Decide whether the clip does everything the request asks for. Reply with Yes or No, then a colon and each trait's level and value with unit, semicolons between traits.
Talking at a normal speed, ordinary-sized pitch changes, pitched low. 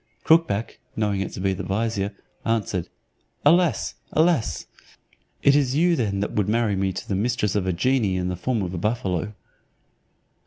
Yes: average, 170 wpm; average, 4.6 semitones; low, 105 Hz